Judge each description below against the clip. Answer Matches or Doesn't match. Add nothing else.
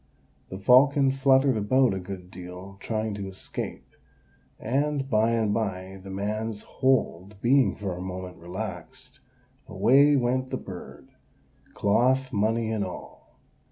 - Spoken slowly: Matches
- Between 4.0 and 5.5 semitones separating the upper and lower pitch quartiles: Matches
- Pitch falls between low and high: Doesn't match